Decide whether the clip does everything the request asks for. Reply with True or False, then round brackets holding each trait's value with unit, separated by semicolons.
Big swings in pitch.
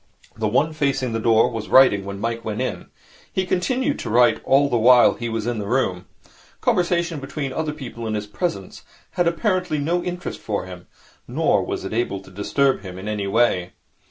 True (6.6 semitones)